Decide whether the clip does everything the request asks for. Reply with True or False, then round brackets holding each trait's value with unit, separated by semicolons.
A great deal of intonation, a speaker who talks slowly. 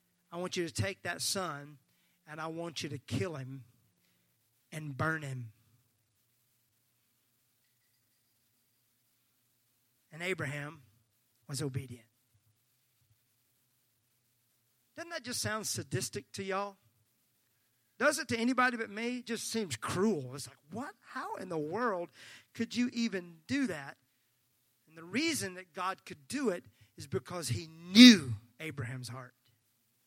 True (6.8 semitones; 130 wpm)